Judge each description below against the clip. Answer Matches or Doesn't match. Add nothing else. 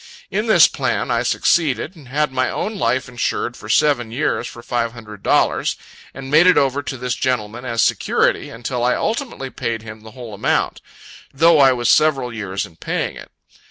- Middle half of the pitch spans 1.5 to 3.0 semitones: Doesn't match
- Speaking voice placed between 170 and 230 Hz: Doesn't match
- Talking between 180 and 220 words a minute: Matches